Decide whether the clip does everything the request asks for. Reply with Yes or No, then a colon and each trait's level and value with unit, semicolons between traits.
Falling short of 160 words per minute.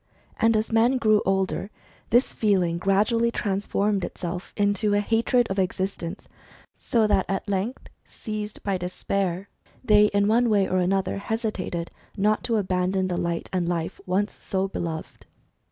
Yes: average, 150 wpm